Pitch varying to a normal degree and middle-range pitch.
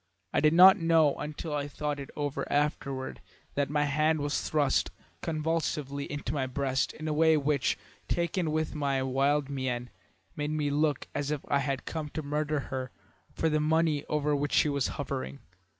No: narrow, 1.8 semitones; medium, 145 Hz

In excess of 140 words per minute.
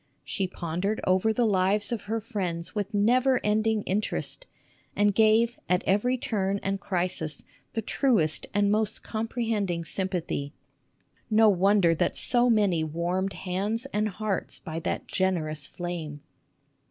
No: slow, 135 wpm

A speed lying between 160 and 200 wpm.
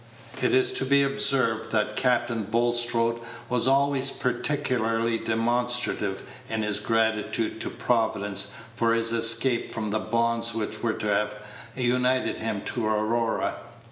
No: slow, 135 wpm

